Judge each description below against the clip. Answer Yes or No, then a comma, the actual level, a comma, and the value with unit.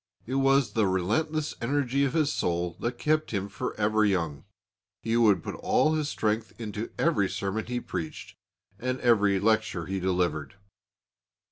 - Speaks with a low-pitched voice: Yes, low, 110 Hz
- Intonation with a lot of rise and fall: Yes, wide, 5.7 semitones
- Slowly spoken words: No, average, 155 wpm